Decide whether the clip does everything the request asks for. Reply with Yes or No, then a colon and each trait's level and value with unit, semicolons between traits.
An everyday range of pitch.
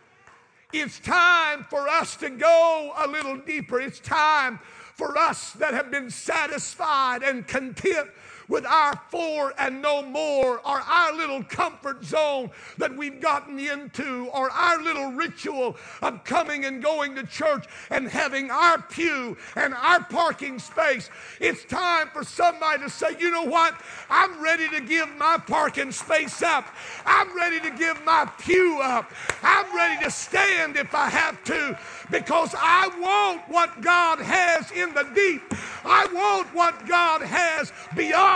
Yes: average, 3.4 semitones